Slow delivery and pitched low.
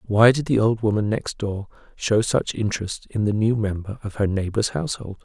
No: fast, 205 wpm; low, 105 Hz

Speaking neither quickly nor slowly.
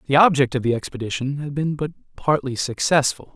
Yes: average, 180 wpm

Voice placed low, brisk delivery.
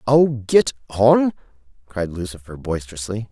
No: low, 110 Hz; slow, 110 wpm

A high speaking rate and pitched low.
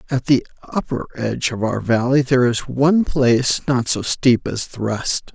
No: average, 190 wpm; low, 125 Hz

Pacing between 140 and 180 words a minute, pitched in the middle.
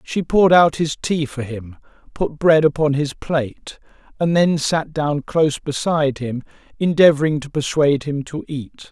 Yes: average, 170 wpm; medium, 150 Hz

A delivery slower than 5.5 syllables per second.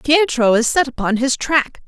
Yes: 4.6 syllables/s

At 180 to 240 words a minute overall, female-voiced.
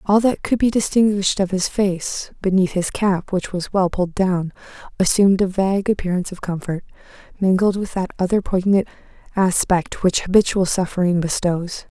No: average, 160 wpm; female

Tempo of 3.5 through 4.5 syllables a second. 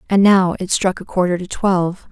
No: 5.3 syllables/s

